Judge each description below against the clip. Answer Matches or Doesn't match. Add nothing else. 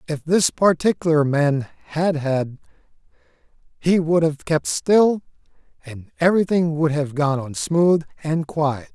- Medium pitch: Matches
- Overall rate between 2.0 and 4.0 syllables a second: Matches